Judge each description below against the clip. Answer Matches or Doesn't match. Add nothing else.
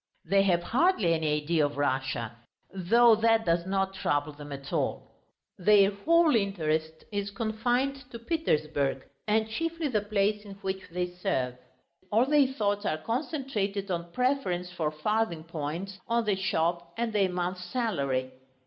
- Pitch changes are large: Matches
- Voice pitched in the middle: Doesn't match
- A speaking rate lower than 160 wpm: Matches